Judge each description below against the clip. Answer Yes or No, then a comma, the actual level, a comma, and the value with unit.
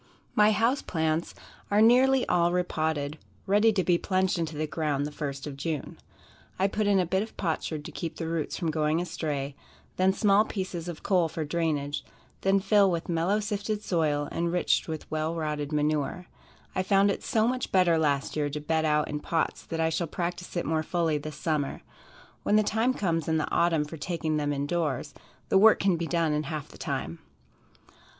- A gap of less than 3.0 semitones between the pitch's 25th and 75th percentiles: No, average, 3.9 semitones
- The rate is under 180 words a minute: No, average, 200 wpm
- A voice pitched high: No, medium, 165 Hz